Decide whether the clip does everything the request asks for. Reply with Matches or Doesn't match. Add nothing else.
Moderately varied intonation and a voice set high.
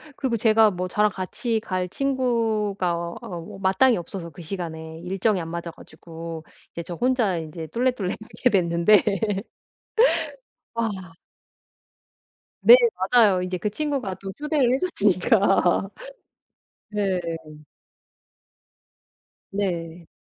Matches